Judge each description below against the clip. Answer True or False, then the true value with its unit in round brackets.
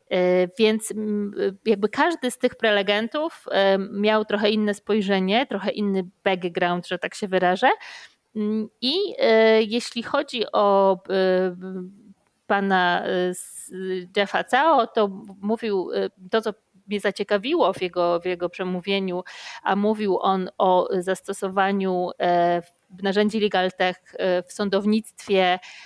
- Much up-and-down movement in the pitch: False (2.5 semitones)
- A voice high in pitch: True (195 Hz)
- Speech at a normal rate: False (105 wpm)